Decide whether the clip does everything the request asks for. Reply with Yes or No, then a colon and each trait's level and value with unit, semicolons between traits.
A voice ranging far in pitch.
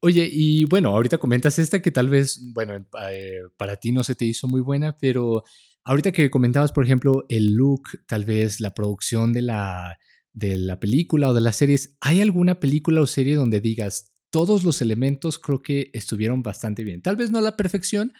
Yes: wide, 5.8 semitones